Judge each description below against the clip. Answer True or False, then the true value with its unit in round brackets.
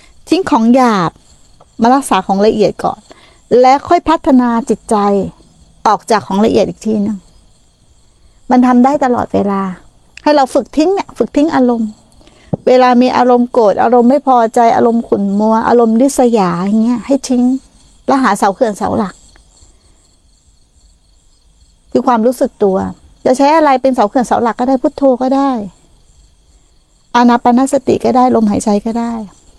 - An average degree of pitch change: True (4.8 semitones)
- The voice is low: False (235 Hz)